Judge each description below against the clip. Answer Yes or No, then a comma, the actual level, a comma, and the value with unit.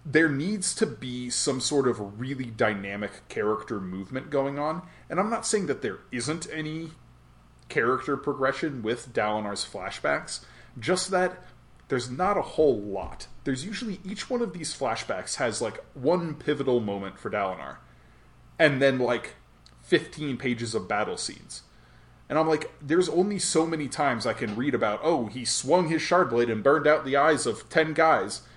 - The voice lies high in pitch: No, medium, 140 Hz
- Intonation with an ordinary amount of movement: No, wide, 5.9 semitones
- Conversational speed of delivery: Yes, average, 170 wpm